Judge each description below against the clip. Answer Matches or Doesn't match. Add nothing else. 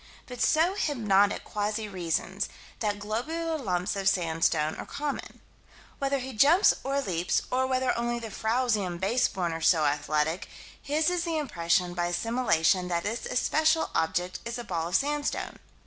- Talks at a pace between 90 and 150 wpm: Doesn't match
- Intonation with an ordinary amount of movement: Doesn't match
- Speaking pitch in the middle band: Doesn't match